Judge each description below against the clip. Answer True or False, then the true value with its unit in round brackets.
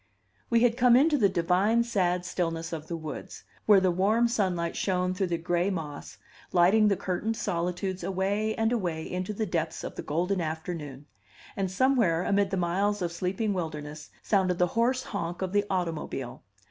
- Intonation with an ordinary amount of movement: True (3.4 semitones)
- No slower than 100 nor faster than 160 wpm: False (175 wpm)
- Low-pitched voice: False (185 Hz)